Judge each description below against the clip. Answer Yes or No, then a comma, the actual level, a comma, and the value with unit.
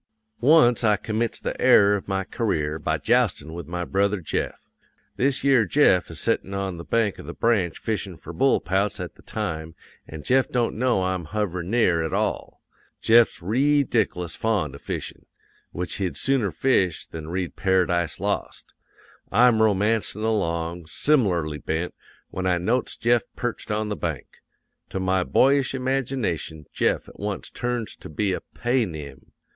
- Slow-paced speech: No, average, 160 wpm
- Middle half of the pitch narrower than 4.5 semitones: No, wide, 5.4 semitones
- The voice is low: Yes, low, 100 Hz